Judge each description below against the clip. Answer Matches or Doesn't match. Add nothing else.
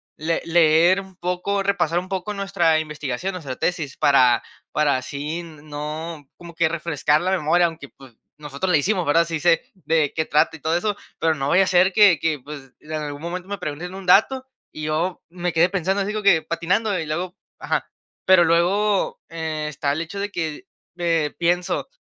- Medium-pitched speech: Matches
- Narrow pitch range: Doesn't match